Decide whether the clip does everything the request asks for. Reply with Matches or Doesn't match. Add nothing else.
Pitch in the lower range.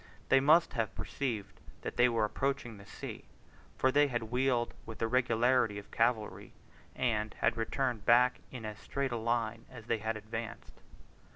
Matches